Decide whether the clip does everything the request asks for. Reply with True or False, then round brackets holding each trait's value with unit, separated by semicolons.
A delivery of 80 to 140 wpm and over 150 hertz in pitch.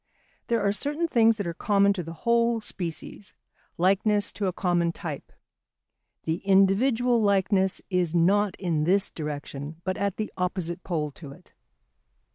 False (150 wpm; 190 Hz)